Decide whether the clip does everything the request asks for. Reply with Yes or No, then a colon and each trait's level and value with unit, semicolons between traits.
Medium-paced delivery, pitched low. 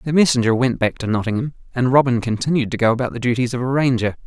No: fast, 240 wpm; low, 125 Hz